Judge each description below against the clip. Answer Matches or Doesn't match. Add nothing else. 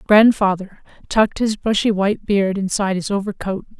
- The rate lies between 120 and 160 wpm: Matches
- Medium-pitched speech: Doesn't match